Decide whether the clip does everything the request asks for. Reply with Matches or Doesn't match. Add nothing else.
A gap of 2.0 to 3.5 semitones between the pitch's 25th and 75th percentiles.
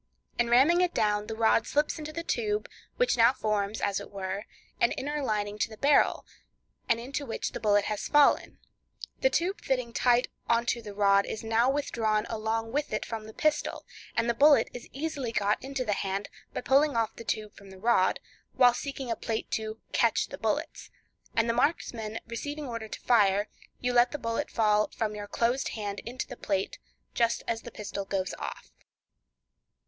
Doesn't match